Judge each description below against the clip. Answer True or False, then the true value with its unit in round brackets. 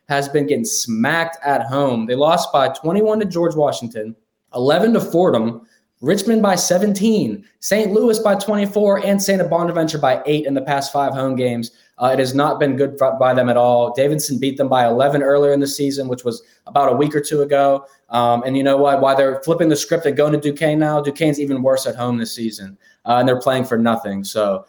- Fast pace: True (220 wpm)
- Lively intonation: False (4.5 semitones)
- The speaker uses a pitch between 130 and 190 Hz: True (140 Hz)